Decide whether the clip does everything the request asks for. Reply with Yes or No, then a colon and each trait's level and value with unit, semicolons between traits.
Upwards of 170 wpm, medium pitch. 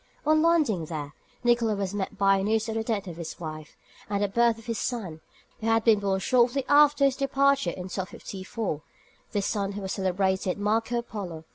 No: average, 200 wpm; high, 205 Hz